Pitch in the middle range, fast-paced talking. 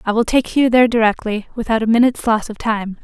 No: high, 225 Hz; fast, 240 wpm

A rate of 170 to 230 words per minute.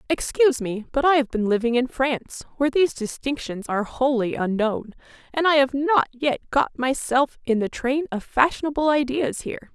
Yes: average, 180 wpm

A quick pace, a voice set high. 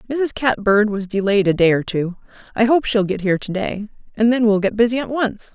Yes: fast, 240 wpm; high, 215 Hz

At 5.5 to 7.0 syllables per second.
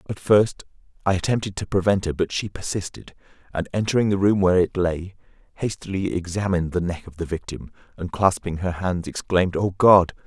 Yes: 5.7 syllables/s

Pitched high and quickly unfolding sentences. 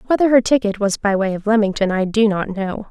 Yes: high, 210 Hz; fast, 250 wpm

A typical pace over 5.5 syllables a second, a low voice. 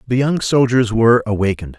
Yes: 6.4 syllables/s; low, 115 Hz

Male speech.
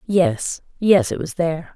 No: female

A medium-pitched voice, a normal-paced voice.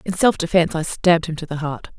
No: medium, 170 Hz; fast, 270 wpm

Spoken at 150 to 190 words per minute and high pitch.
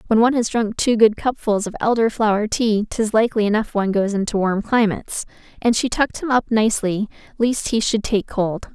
No: fast, 205 wpm; high, 220 Hz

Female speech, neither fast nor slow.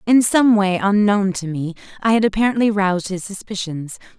Yes: female; average, 170 wpm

